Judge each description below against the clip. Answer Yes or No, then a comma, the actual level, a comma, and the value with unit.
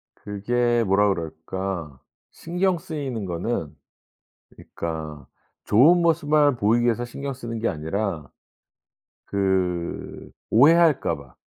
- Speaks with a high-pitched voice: No, low, 110 Hz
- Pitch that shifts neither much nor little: No, wide, 8.1 semitones